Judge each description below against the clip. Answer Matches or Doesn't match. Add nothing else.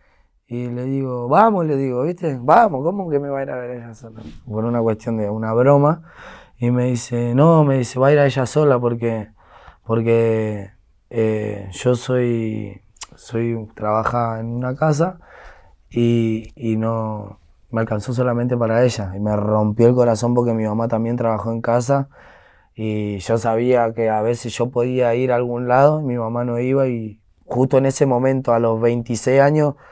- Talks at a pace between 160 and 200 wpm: Matches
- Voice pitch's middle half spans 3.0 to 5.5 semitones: Doesn't match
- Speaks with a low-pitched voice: Matches